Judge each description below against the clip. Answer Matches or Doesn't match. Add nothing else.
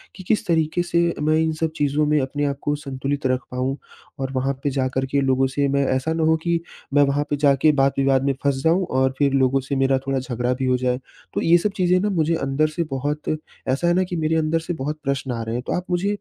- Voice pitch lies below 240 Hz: Matches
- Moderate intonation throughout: Matches